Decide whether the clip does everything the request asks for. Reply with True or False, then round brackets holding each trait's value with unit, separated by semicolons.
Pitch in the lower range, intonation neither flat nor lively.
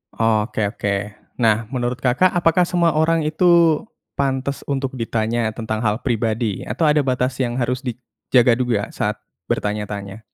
True (125 Hz; 4.1 semitones)